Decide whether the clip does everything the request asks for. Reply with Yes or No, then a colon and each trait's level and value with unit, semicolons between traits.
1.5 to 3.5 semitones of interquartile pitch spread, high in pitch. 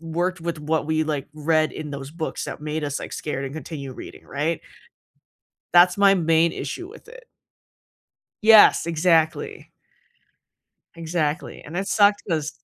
No: average, 2.8 semitones; medium, 160 Hz